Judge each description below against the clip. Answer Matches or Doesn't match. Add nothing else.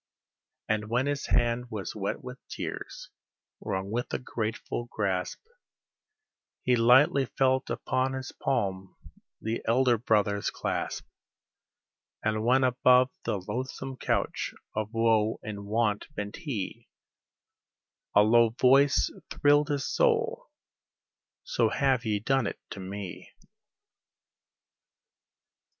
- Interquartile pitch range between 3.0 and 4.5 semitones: Matches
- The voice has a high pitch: Doesn't match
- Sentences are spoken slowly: Matches